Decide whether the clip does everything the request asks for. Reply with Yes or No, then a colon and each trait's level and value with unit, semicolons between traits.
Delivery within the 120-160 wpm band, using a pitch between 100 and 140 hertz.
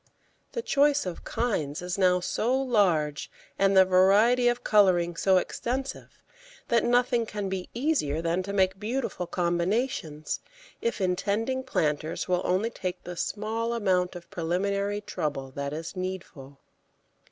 No: average, 140 wpm; high, 190 Hz